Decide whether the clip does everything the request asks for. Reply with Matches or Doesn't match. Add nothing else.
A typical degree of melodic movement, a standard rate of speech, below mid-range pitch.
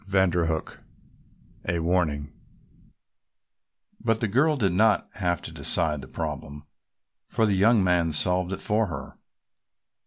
Doesn't match